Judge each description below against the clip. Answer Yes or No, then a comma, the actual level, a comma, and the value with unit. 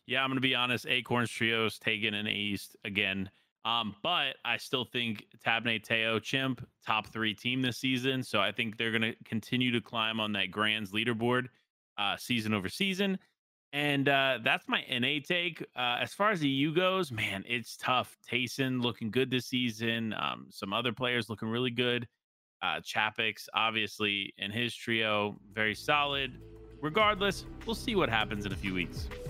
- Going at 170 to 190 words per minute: Yes, average, 175 wpm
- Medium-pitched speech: No, low, 120 Hz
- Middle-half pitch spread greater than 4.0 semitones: No, average, 3.2 semitones